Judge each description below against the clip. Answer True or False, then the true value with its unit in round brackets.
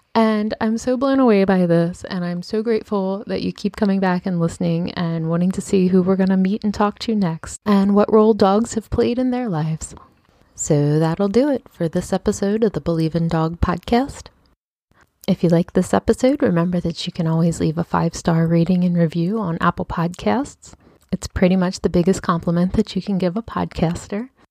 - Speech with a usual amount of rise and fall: True (4.0 semitones)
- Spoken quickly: True (210 wpm)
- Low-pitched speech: False (185 Hz)